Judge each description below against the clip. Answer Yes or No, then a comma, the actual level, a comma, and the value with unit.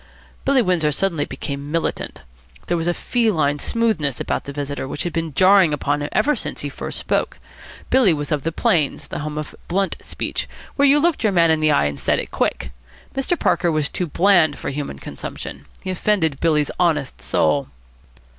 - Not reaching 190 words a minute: No, average, 195 wpm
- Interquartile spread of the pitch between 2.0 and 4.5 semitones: No, average, 5.0 semitones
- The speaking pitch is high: No, medium, 160 Hz